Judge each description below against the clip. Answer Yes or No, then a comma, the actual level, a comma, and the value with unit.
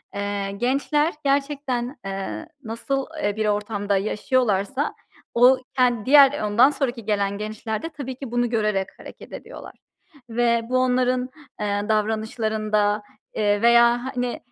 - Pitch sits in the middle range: No, high, 235 Hz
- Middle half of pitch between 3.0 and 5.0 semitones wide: Yes, average, 3.5 semitones